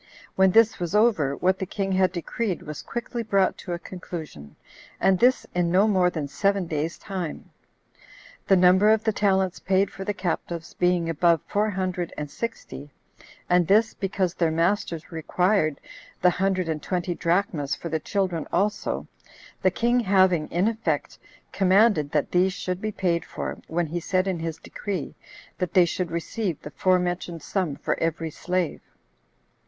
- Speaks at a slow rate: No, average, 165 wpm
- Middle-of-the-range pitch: Yes, medium, 180 Hz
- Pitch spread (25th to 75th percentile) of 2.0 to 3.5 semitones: Yes, average, 2.8 semitones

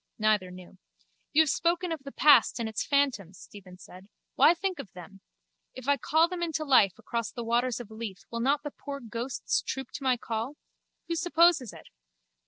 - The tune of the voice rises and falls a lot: Yes, wide, 5.8 semitones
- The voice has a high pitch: Yes, very high, 255 Hz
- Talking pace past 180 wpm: Yes, average, 190 wpm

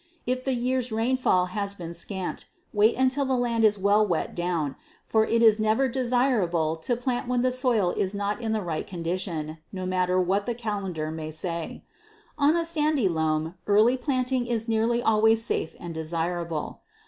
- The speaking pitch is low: No, high, 215 Hz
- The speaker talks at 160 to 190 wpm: Yes, average, 175 wpm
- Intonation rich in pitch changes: Yes, wide, 5.7 semitones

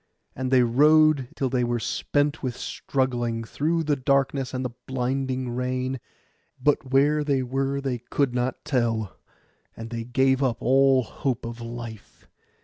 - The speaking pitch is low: Yes, low, 130 Hz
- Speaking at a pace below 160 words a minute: Yes, average, 150 wpm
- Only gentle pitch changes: Yes, narrow, 2.2 semitones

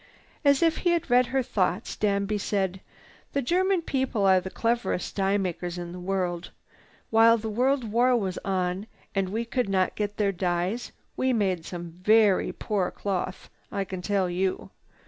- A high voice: Yes, high, 200 Hz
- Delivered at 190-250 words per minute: No, average, 170 wpm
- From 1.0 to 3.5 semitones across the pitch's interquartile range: No, average, 4.2 semitones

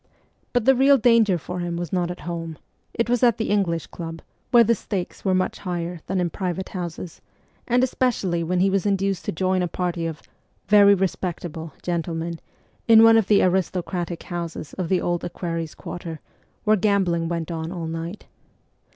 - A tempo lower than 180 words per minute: No, average, 190 wpm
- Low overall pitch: No, medium, 180 Hz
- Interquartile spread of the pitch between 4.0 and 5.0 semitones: No, average, 3.0 semitones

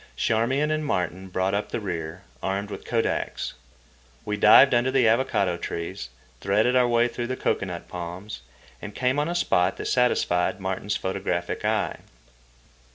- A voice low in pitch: Yes, low, 105 Hz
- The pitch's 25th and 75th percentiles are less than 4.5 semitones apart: No, average, 5.1 semitones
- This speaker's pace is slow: No, average, 155 wpm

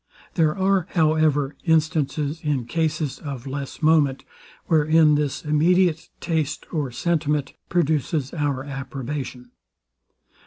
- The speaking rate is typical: No, slow, 105 wpm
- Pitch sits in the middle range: Yes, medium, 150 Hz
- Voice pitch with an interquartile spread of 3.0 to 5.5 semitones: No, narrow, 2.6 semitones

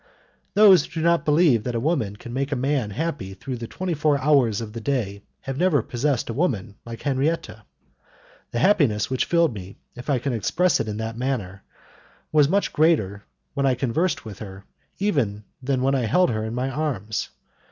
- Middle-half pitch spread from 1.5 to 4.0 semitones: No, wide, 5.4 semitones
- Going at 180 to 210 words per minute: Yes, average, 195 wpm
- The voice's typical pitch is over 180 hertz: No, low, 130 Hz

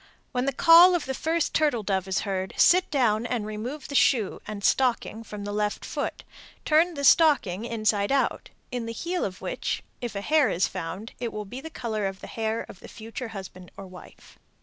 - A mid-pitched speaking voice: No, high, 225 Hz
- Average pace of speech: No, fast, 215 wpm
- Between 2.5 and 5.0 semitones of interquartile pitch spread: No, wide, 5.4 semitones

